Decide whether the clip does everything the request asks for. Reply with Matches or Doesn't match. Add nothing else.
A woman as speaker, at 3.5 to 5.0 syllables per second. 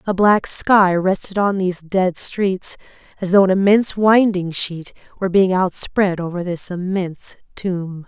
Matches